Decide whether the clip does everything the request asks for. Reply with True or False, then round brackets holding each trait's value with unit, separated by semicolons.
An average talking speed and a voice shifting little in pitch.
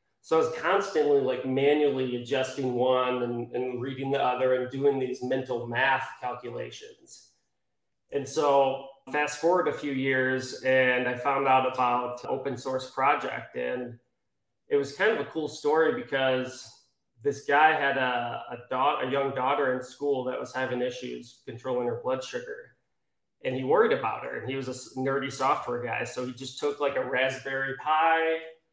True (170 wpm; 1.9 semitones)